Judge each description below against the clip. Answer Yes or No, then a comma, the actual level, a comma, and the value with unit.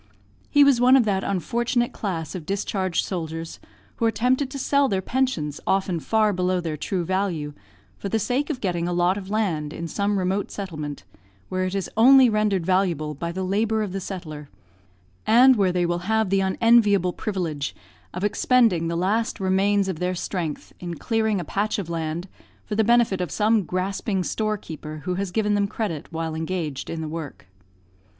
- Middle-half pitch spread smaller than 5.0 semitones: Yes, average, 4.1 semitones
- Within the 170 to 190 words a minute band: Yes, average, 185 wpm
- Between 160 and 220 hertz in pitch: Yes, high, 190 Hz